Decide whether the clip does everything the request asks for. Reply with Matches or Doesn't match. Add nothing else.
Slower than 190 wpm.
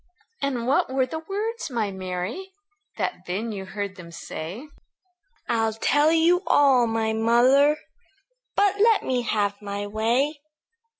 Matches